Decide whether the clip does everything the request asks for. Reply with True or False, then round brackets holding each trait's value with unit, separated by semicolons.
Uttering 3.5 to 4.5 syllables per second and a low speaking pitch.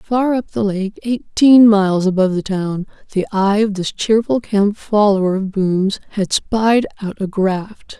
False (4.1 syllables/s; 205 Hz)